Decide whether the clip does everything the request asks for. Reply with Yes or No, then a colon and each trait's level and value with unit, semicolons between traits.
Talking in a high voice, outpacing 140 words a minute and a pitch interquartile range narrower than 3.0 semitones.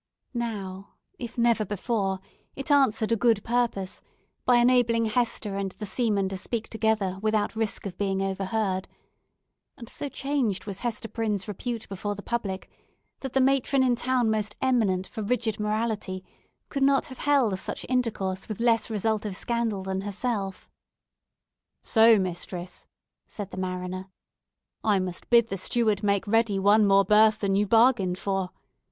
No: high, 215 Hz; average, 155 wpm; average, 3.4 semitones